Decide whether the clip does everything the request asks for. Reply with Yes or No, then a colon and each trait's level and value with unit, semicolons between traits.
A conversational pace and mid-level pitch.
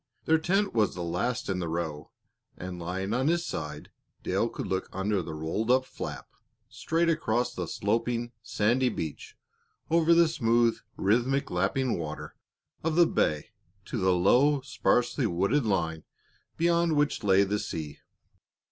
No: average, 150 wpm; low, 115 Hz